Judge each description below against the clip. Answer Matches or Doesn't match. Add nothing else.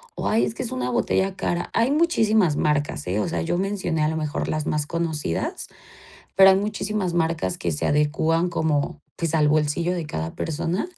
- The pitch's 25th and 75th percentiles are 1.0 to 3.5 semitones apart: Doesn't match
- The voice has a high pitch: Doesn't match